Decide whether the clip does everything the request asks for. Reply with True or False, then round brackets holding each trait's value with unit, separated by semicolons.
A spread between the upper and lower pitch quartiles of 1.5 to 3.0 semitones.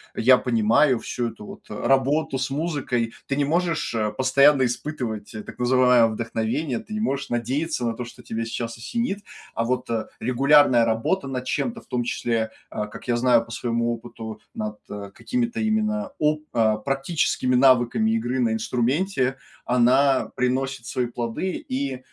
False (3.5 semitones)